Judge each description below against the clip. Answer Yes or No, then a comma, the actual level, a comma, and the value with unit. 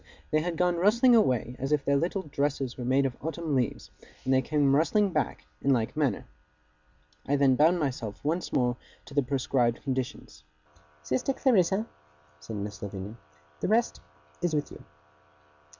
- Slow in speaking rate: No, average, 165 wpm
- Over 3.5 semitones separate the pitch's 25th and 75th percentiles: Yes, average, 5.2 semitones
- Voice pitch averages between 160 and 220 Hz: No, medium, 140 Hz